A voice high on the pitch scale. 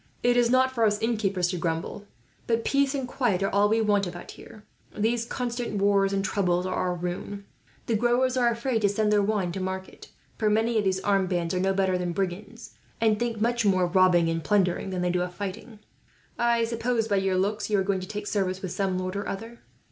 Yes: high, 200 Hz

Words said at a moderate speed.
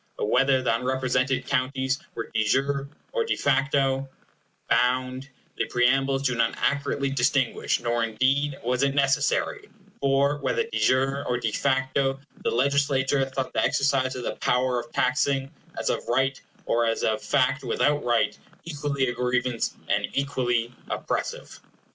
Yes: average, 150 wpm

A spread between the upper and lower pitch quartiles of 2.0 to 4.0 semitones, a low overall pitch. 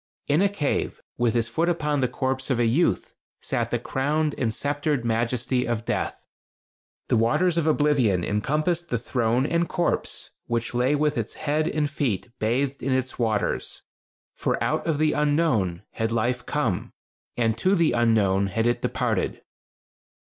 No: average, 4.7 semitones; low, 130 Hz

